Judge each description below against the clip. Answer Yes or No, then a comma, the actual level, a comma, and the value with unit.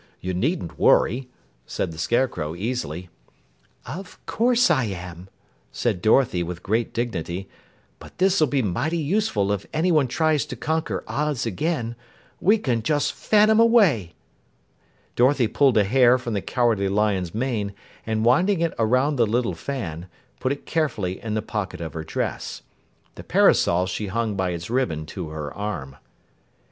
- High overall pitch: No, low, 115 Hz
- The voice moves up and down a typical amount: No, wide, 7.6 semitones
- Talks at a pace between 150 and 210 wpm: Yes, average, 155 wpm